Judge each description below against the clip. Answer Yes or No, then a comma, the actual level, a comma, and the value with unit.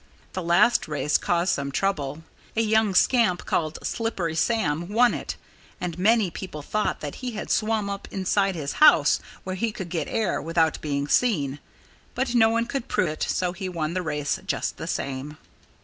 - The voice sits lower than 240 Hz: Yes, medium, 185 Hz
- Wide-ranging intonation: Yes, wide, 5.9 semitones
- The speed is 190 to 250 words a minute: No, average, 180 wpm